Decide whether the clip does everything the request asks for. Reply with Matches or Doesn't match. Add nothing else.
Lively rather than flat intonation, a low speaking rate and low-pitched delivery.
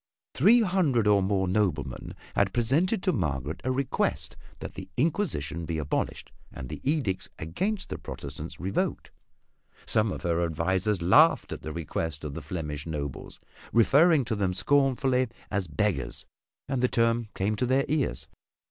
Doesn't match